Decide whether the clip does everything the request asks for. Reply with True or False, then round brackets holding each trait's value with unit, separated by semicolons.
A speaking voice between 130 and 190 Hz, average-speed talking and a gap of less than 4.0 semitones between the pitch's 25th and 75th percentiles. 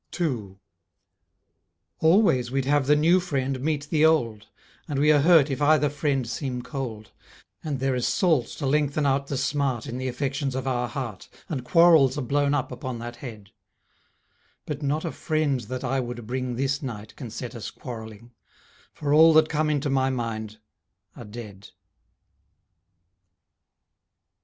True (135 Hz; 160 wpm; 3.4 semitones)